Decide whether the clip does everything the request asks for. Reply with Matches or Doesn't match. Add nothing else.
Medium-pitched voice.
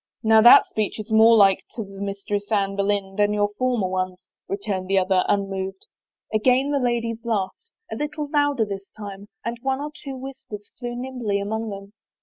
Doesn't match